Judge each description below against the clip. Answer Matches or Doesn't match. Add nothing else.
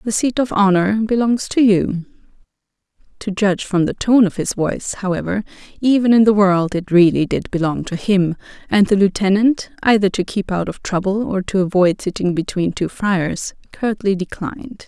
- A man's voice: Doesn't match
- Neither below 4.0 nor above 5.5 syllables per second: Matches